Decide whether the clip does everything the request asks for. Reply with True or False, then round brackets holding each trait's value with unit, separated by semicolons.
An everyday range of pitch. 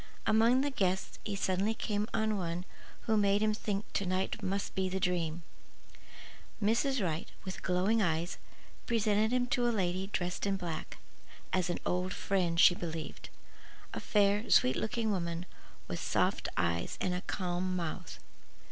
True (3.3 semitones)